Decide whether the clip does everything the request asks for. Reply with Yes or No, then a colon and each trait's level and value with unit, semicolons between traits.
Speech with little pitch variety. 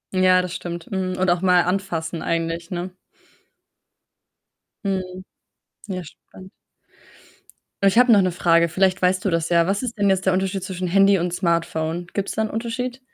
Yes: narrow, 2.1 semitones